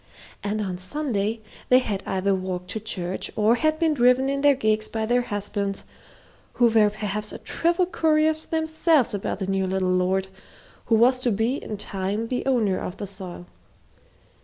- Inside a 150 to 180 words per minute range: Yes, average, 175 wpm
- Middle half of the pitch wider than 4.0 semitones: Yes, average, 5.0 semitones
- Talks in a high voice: Yes, high, 215 Hz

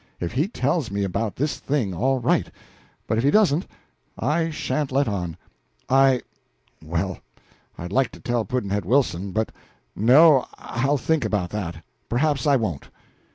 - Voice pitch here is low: Yes, low, 125 Hz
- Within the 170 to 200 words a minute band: No, average, 155 wpm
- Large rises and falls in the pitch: Yes, wide, 6.2 semitones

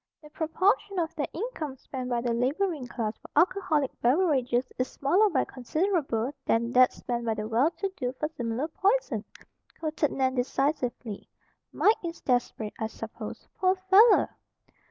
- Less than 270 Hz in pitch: No, very high, 280 Hz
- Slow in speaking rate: No, average, 155 wpm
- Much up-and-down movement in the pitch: Yes, wide, 6.1 semitones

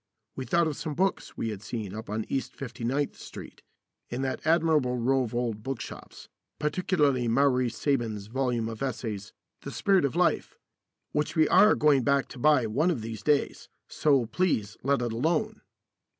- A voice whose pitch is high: No, low, 130 Hz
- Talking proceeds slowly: No, average, 175 wpm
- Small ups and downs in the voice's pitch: No, average, 4.7 semitones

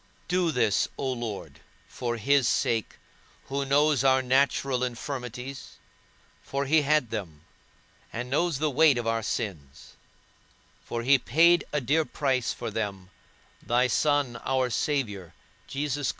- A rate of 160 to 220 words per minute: No, slow, 135 wpm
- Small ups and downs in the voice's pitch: No, average, 3.4 semitones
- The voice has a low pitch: Yes, low, 130 Hz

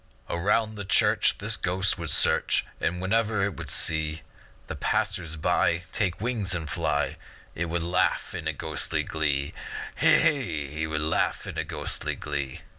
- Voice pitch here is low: Yes, very low, 85 Hz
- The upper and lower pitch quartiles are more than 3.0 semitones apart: Yes, average, 3.7 semitones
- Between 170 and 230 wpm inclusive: No, average, 155 wpm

